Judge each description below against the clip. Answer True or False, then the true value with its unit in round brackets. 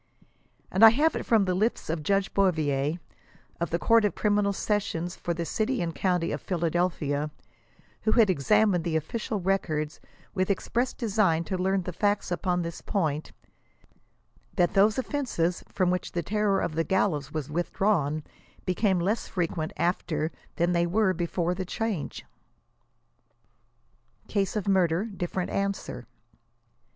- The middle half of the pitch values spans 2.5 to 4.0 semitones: True (3.6 semitones)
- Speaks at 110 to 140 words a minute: False (150 wpm)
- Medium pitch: True (180 Hz)